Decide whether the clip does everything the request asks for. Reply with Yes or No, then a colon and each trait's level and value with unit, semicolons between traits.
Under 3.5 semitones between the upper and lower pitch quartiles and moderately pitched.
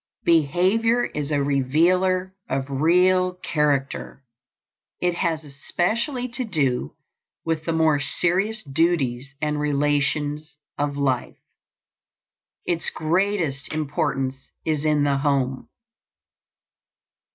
No: average, 4.3 semitones; medium, 150 Hz